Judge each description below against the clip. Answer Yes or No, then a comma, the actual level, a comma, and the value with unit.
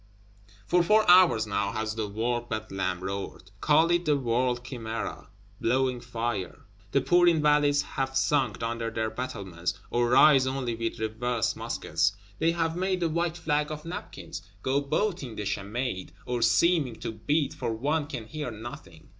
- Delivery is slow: No, average, 160 wpm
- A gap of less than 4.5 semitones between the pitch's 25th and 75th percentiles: No, average, 5.3 semitones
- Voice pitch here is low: Yes, low, 125 Hz